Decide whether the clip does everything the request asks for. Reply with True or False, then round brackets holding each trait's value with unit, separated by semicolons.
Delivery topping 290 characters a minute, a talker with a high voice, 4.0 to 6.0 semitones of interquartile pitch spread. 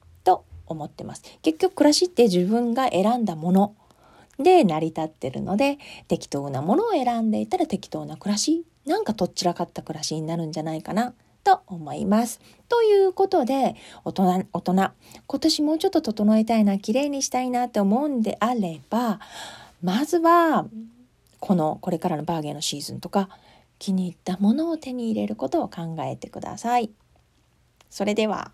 False (340 characters per minute; 210 Hz; 7.5 semitones)